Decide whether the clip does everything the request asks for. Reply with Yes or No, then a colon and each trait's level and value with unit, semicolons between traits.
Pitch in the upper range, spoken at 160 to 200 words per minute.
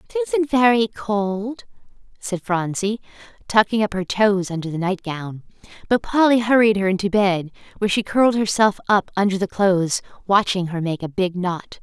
Yes: high, 205 Hz; average, 165 wpm